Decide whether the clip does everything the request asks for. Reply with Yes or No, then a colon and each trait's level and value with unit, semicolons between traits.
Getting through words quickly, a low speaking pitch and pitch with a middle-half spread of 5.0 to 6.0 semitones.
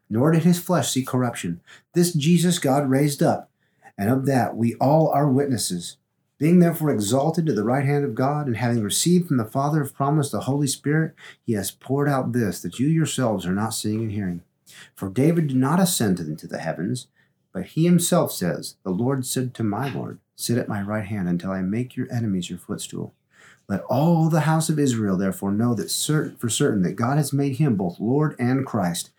Yes: fast, 210 wpm; low, 130 Hz; average, 5.3 semitones